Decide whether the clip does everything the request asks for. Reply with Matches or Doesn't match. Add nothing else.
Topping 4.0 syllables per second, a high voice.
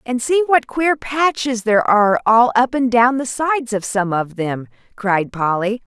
Matches